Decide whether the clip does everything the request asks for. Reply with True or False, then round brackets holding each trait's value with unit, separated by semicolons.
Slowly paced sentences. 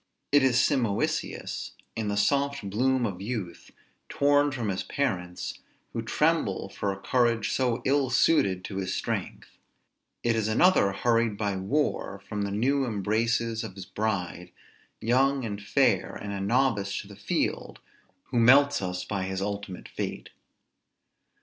False (150 wpm)